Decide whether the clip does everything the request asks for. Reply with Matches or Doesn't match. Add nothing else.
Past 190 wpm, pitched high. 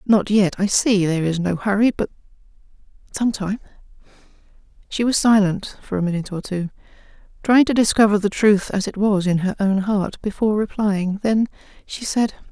Doesn't match